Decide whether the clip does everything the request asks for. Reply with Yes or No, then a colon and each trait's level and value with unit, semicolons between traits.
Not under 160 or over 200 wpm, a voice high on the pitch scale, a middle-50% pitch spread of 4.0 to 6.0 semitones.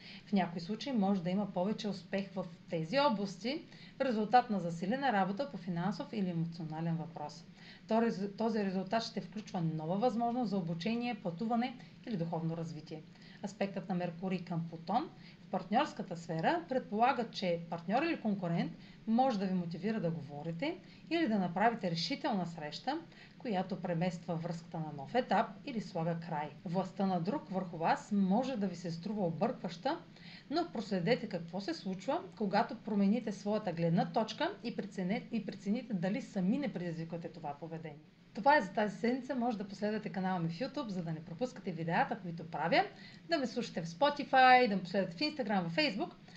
Yes: fast, 165 wpm; high, 195 Hz; average, 4.6 semitones